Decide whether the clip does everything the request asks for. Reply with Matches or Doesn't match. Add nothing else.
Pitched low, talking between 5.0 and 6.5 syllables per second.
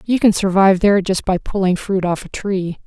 Doesn't match